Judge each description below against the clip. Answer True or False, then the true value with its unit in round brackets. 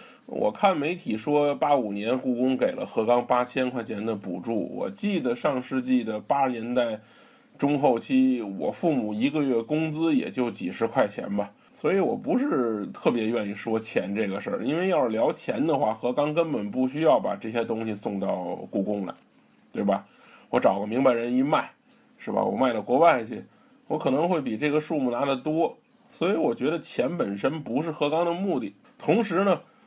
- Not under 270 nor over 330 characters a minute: True (275 characters per minute)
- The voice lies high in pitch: False (130 Hz)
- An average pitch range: False (5.7 semitones)